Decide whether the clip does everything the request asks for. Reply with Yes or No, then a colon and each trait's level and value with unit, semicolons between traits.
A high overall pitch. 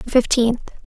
Yes: high, 240 Hz